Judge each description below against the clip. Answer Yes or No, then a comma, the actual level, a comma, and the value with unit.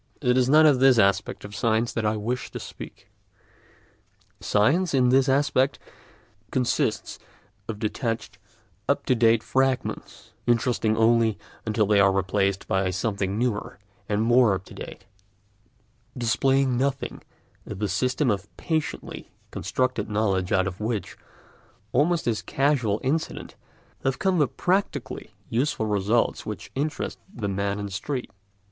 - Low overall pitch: Yes, low, 115 Hz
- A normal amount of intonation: Yes, average, 4.3 semitones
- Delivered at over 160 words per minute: No, average, 140 wpm